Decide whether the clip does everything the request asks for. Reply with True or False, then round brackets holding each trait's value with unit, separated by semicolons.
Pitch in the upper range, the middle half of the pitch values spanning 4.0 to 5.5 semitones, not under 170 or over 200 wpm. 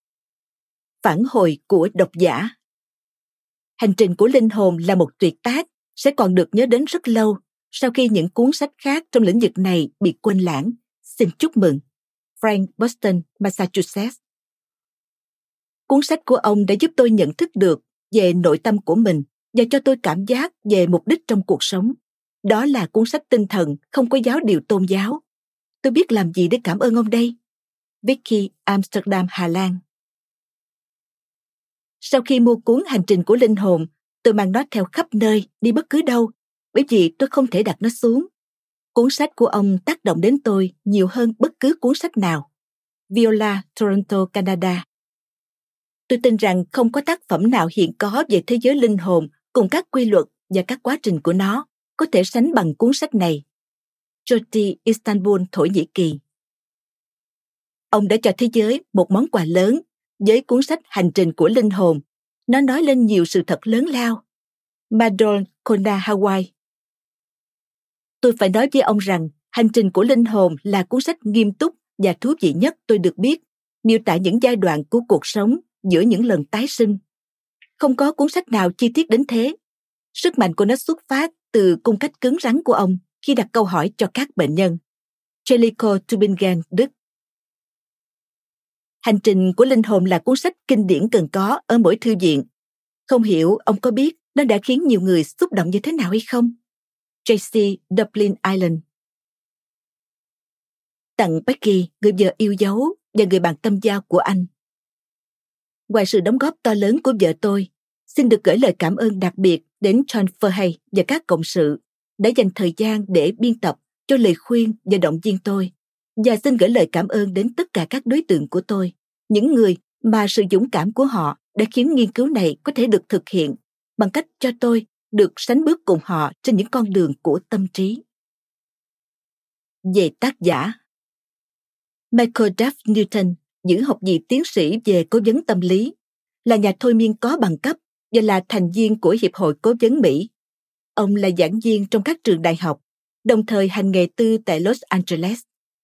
True (215 Hz; 4.7 semitones; 185 wpm)